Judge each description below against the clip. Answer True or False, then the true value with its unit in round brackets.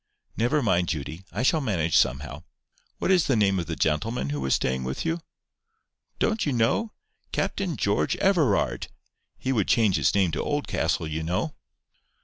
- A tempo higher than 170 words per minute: False (160 wpm)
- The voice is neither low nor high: False (100 Hz)